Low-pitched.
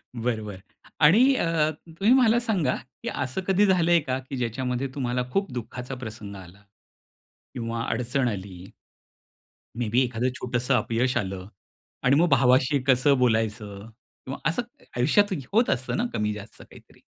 Yes: low, 125 Hz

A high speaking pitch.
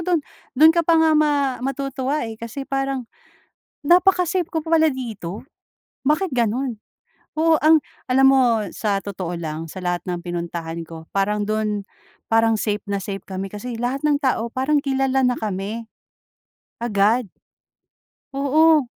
Yes: very high, 250 Hz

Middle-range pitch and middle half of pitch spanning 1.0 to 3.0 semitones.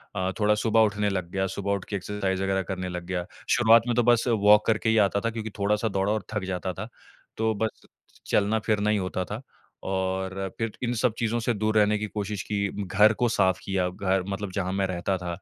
No: low, 100 Hz; narrow, 2.4 semitones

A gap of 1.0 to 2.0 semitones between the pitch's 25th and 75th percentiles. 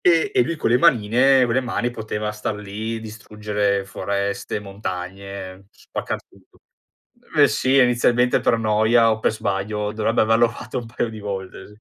No: average, 2.9 semitones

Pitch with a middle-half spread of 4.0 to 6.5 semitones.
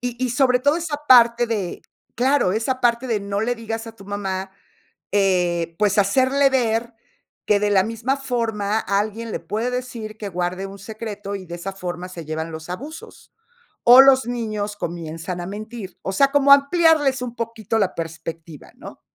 Yes: average, 4.4 semitones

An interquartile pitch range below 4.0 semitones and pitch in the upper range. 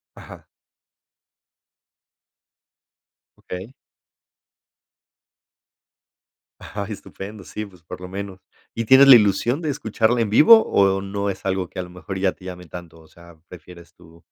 No: average, 3.2 semitones; very low, 95 Hz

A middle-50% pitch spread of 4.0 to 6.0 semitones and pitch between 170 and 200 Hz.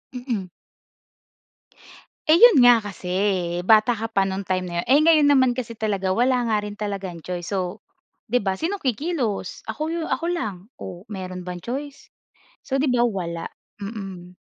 No: average, 5.3 semitones; high, 215 Hz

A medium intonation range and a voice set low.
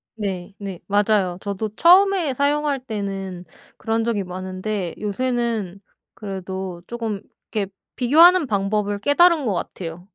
No: average, 4.5 semitones; high, 205 Hz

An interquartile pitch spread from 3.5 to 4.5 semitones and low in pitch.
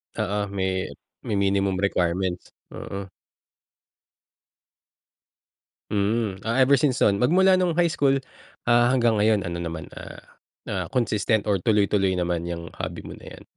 Yes: average, 4.2 semitones; low, 100 Hz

